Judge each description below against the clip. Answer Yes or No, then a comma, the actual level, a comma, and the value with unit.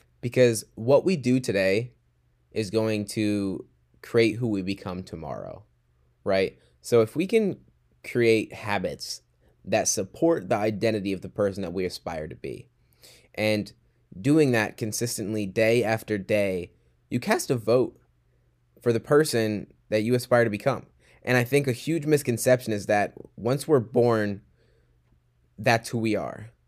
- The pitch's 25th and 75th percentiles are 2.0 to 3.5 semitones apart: No, average, 4.7 semitones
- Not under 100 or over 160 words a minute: Yes, average, 150 wpm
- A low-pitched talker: Yes, low, 110 Hz